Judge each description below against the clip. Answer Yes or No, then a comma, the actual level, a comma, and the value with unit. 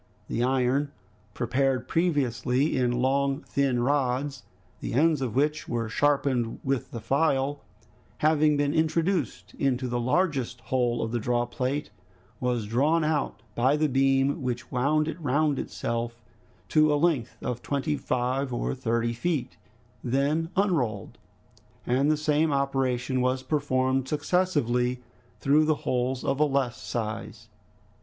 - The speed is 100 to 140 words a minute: Yes, slow, 135 wpm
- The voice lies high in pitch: No, low, 135 Hz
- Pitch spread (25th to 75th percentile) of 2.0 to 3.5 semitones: Yes, average, 3.1 semitones